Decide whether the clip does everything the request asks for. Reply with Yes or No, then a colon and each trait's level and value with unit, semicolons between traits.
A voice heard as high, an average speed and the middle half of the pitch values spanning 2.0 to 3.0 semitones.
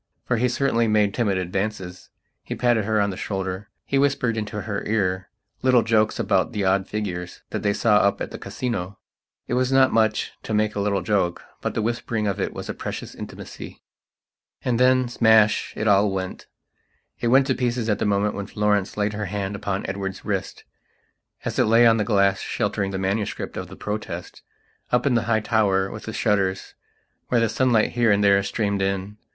No: low, 105 Hz; average, 190 wpm; average, 2.7 semitones